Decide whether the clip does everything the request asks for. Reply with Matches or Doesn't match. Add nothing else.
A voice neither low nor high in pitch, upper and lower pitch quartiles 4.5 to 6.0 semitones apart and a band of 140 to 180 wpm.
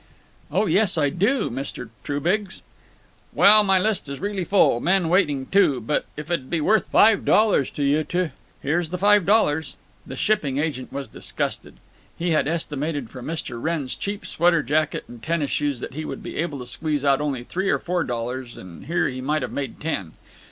Doesn't match